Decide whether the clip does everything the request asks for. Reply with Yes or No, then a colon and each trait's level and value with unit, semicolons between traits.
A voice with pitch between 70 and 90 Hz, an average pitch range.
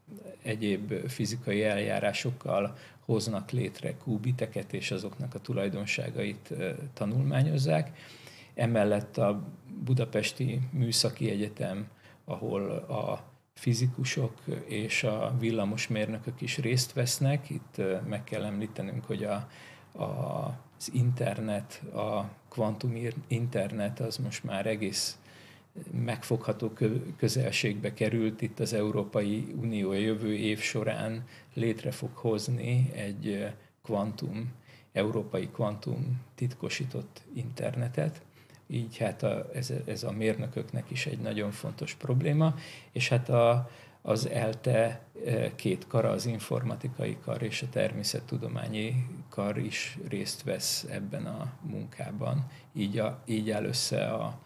No: low, 120 Hz; average, 3.4 semitones